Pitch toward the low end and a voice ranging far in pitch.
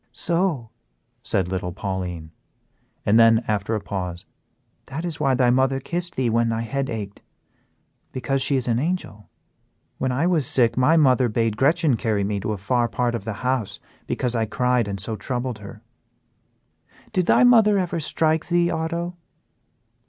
Yes: low, 125 Hz; wide, 6.1 semitones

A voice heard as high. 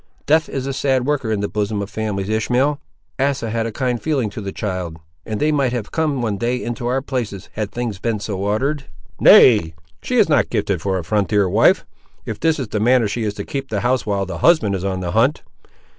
No: low, 115 Hz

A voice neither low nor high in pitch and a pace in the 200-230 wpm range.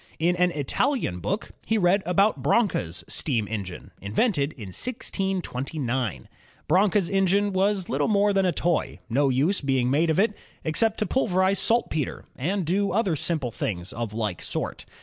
No: medium, 175 Hz; average, 155 wpm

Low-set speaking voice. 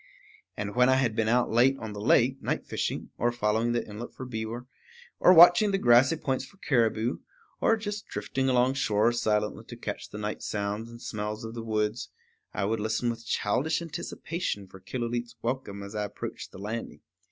Yes: low, 115 Hz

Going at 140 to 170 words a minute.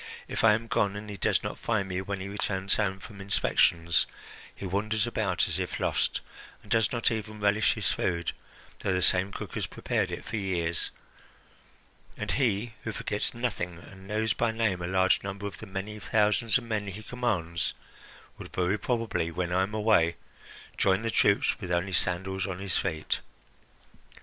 No: average, 180 wpm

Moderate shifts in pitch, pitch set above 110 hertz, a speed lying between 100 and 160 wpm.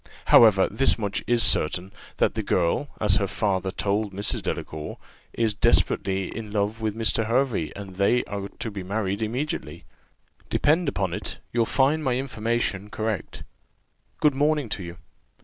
No: average, 3.5 semitones; low, 105 Hz; average, 155 wpm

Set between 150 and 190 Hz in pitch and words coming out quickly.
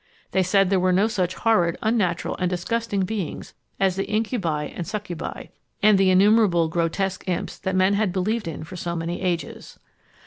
No: medium, 185 Hz; average, 175 wpm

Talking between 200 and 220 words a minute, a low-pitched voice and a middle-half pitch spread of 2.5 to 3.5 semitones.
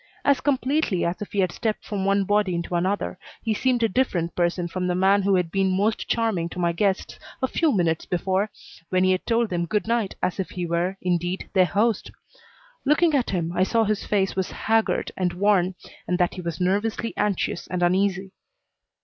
No: fast, 205 wpm; high, 190 Hz; average, 3.2 semitones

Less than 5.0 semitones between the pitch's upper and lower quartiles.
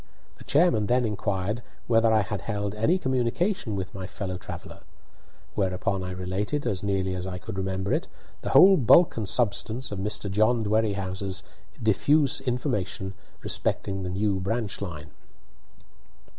Yes: average, 3.6 semitones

